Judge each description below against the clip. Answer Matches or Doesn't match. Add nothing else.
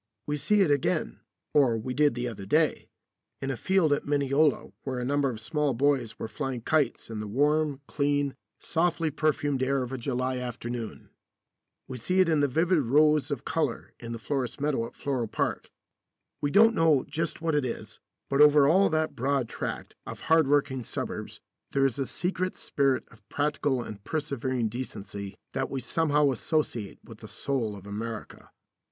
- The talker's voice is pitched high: Doesn't match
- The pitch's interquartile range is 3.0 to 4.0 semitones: Matches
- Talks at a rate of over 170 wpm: Matches